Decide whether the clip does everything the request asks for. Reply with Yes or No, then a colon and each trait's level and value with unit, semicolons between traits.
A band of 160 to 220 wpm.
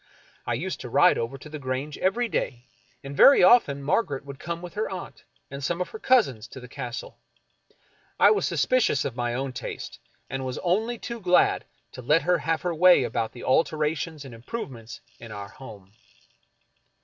Yes: average, 190 wpm